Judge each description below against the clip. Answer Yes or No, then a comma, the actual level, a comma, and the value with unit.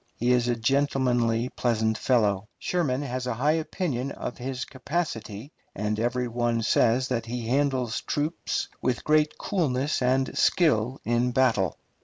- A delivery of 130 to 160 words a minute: Yes, average, 145 wpm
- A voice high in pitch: No, low, 125 Hz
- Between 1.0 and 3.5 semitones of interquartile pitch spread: Yes, average, 2.8 semitones